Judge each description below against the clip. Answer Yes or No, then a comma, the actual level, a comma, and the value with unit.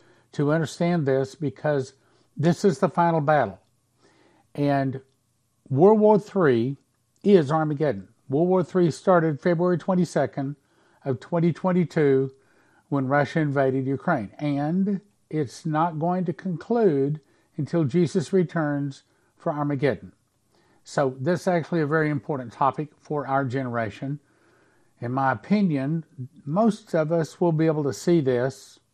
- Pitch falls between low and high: Yes, medium, 150 Hz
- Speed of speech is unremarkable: No, slow, 125 wpm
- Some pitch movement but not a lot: Yes, average, 4.3 semitones